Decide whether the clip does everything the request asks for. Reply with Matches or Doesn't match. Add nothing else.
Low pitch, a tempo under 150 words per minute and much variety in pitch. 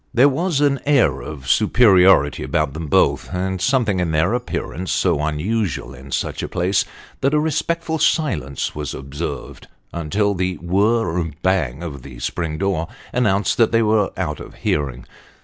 Doesn't match